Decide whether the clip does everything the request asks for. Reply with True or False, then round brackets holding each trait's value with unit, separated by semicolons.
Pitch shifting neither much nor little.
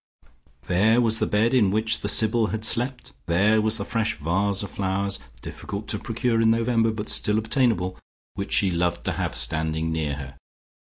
True (3.4 semitones)